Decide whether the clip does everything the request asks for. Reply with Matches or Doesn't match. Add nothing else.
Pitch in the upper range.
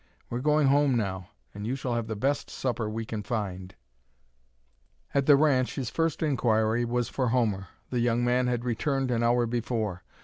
Doesn't match